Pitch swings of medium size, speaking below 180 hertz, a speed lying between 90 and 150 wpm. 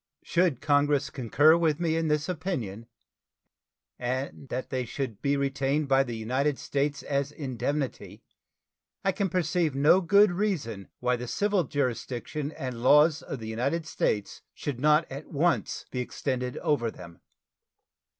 Yes: average, 3.9 semitones; medium, 140 Hz; average, 145 wpm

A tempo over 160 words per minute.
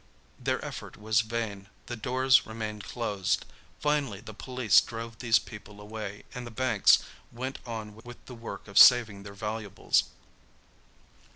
No: average, 145 wpm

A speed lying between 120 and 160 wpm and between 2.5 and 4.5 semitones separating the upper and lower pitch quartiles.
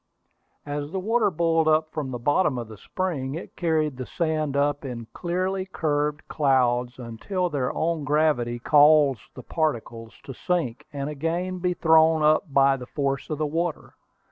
No: average, 170 wpm; average, 3.4 semitones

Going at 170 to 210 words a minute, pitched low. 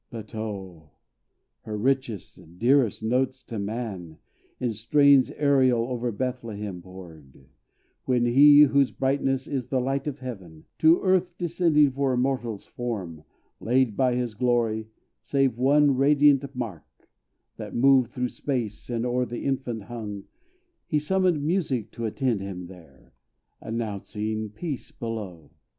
No: slow, 135 wpm; low, 120 Hz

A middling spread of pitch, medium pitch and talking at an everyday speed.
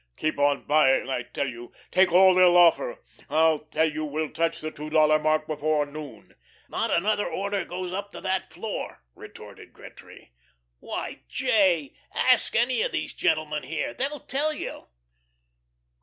Yes: average, 3.9 semitones; medium, 160 Hz; average, 155 wpm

